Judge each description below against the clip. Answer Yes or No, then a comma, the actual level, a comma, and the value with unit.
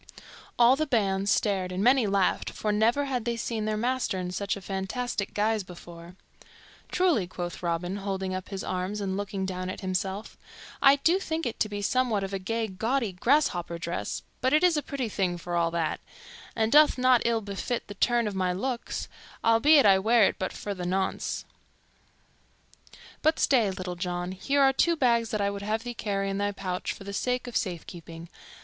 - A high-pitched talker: Yes, high, 205 Hz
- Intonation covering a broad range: No, average, 4.5 semitones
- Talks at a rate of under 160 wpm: No, average, 195 wpm